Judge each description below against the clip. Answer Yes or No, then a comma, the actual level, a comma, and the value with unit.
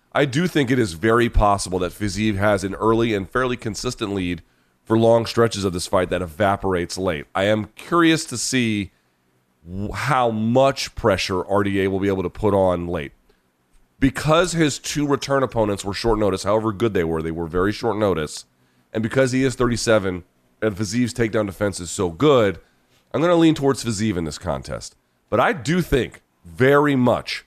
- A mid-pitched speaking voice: No, low, 110 Hz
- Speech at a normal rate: Yes, average, 190 wpm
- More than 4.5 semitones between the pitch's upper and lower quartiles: Yes, wide, 5.4 semitones